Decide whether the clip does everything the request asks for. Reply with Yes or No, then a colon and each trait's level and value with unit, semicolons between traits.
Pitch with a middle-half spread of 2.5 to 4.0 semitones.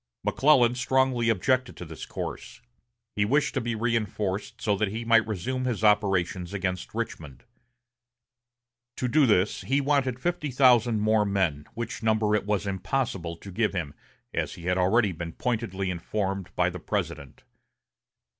No: average, 4.4 semitones